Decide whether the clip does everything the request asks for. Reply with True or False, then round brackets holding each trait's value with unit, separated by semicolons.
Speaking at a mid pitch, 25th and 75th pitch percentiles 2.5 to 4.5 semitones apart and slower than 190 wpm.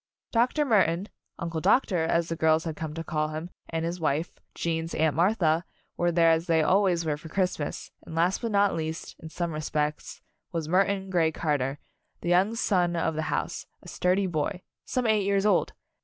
False (170 Hz; 3.0 semitones; 195 wpm)